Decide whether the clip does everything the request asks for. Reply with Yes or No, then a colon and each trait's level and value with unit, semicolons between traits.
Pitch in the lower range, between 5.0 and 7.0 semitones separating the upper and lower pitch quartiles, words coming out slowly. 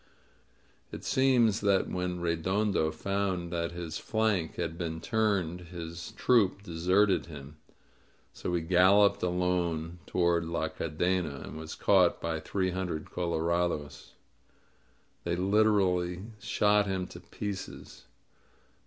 No: very low, 90 Hz; average, 2.8 semitones; slow, 120 wpm